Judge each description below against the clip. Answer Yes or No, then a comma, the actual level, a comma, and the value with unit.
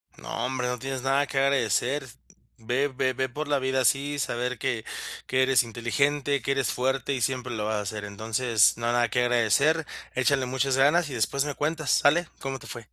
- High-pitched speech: No, low, 130 Hz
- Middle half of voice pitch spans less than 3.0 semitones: Yes, narrow, 2.5 semitones